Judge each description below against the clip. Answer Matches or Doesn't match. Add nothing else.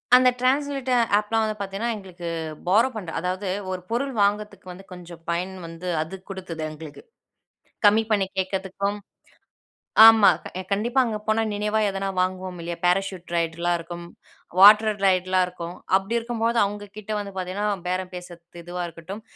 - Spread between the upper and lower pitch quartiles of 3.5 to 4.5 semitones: Doesn't match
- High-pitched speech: Matches